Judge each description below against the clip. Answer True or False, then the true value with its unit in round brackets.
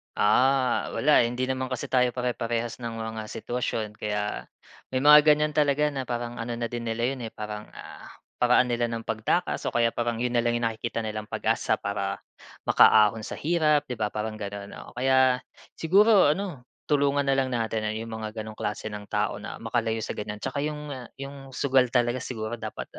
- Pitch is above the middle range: False (120 Hz)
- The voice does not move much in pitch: False (3.2 semitones)